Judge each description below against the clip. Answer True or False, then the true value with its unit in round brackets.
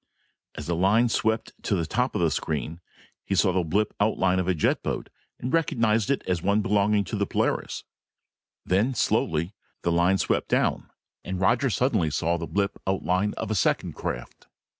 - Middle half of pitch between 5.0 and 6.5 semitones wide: False (4.1 semitones)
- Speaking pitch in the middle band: False (95 Hz)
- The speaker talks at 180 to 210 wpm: True (185 wpm)